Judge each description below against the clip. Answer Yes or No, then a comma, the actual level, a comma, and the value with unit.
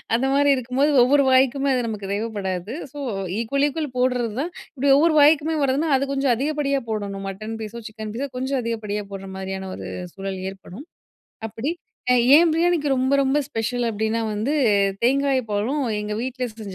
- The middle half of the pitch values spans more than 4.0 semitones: Yes, average, 4.8 semitones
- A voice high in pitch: Yes, very high, 250 Hz